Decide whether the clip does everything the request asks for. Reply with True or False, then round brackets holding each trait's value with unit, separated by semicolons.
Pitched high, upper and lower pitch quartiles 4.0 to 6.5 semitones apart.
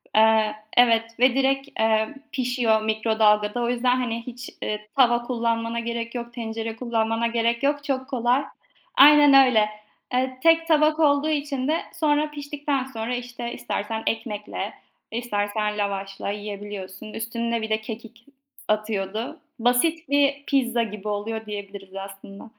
False (235 Hz; 3.1 semitones)